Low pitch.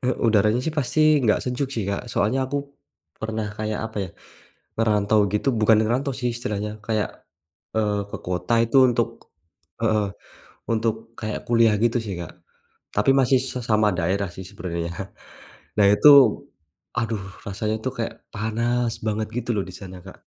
Yes: low, 110 Hz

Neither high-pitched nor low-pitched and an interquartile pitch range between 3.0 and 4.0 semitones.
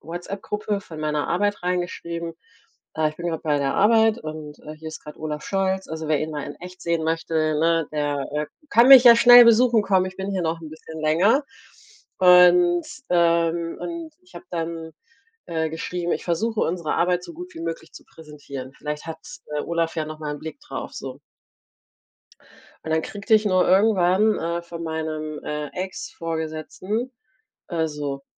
Yes: medium, 170 Hz; average, 3.5 semitones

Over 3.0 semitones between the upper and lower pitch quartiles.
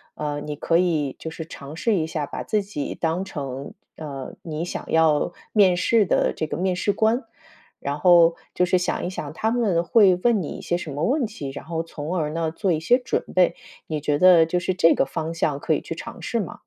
Yes: average, 3.4 semitones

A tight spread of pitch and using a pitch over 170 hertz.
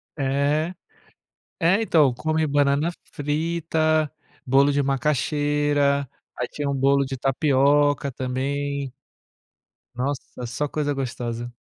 No: narrow, 1.7 semitones; medium, 140 Hz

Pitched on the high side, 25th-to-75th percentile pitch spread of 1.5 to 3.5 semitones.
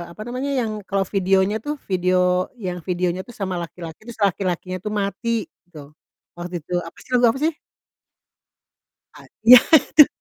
No: high, 195 Hz; average, 4.8 semitones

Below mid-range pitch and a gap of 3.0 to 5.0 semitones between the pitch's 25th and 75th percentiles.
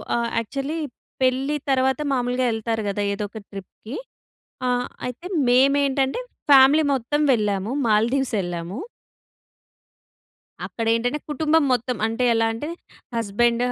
No: high, 245 Hz; average, 3.3 semitones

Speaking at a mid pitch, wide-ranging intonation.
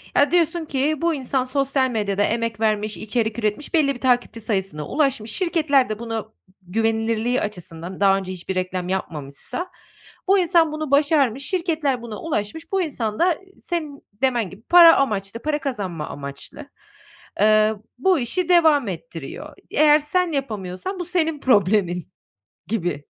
No: high, 245 Hz; wide, 7.0 semitones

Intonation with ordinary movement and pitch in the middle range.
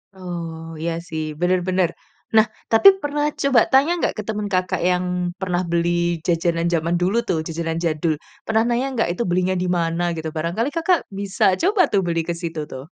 Yes: average, 4.7 semitones; medium, 180 Hz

